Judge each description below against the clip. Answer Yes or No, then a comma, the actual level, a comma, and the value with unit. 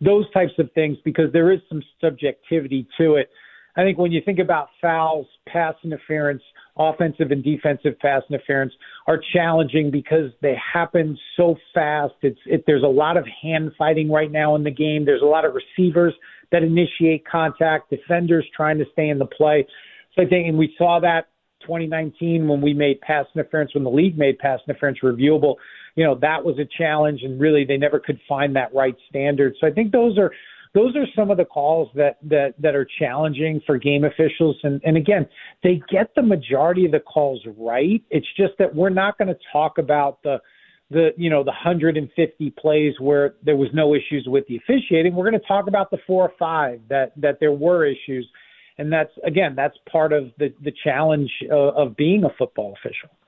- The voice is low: No, medium, 155 Hz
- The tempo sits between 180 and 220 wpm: Yes, average, 200 wpm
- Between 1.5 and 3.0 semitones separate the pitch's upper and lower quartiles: Yes, average, 2.7 semitones